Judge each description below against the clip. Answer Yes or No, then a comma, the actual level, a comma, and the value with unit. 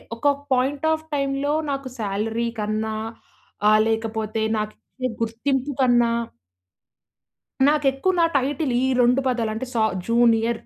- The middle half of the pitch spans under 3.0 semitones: No, average, 3.6 semitones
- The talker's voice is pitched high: Yes, high, 240 Hz